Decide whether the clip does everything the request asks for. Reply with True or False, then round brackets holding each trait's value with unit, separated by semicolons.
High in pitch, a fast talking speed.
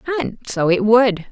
False (225 Hz; 185 wpm)